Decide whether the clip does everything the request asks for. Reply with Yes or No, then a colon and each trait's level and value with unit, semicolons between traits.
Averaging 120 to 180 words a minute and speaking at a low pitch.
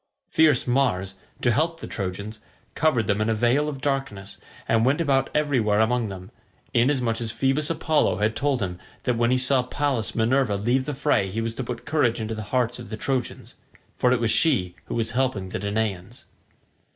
No: average, 190 wpm; low, 120 Hz